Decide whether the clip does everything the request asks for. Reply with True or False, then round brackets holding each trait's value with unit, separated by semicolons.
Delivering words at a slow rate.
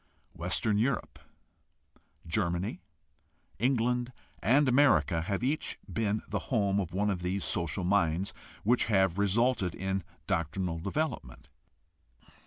True (110 wpm)